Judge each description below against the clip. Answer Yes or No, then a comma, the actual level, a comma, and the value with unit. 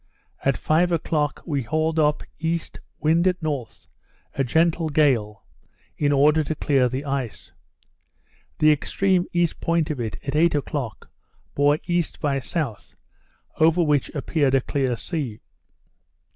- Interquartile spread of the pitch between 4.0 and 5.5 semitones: No, average, 3.1 semitones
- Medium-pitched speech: Yes, medium, 150 Hz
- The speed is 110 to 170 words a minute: Yes, average, 140 wpm